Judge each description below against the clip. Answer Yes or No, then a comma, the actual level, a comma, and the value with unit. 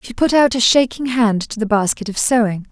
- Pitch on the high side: Yes, high, 230 Hz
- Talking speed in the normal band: No, fast, 245 wpm